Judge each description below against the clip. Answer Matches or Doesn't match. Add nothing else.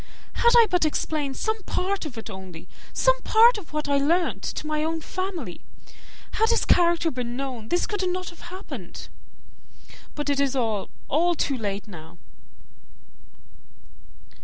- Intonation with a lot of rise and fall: Matches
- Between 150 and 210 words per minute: Matches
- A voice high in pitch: Matches